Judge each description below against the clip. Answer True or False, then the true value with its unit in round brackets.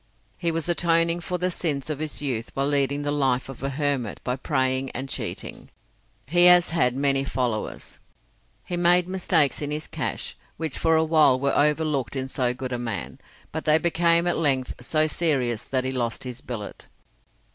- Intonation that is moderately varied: True (4.0 semitones)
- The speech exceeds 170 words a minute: True (185 wpm)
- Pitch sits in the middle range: True (145 Hz)